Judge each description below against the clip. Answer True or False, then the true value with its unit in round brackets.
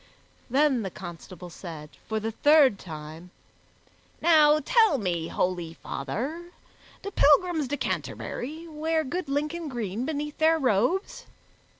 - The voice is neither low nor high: False (275 Hz)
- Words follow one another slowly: True (120 wpm)